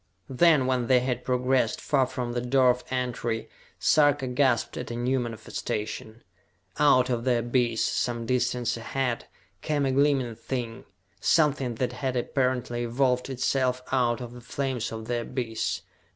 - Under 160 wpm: Yes, average, 150 wpm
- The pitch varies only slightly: Yes, narrow, 1.7 semitones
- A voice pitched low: Yes, low, 125 Hz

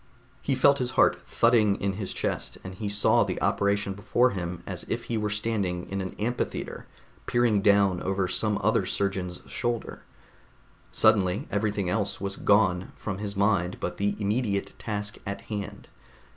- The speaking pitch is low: Yes, low, 100 Hz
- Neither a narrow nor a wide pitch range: No, narrow, 2.1 semitones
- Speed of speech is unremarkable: Yes, average, 160 wpm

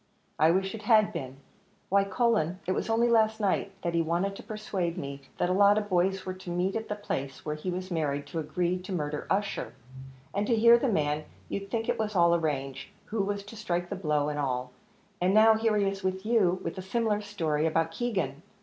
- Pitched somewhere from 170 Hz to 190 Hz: Yes, medium, 185 Hz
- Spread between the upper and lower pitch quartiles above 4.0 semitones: Yes, average, 4.4 semitones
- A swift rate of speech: Yes, fast, 225 wpm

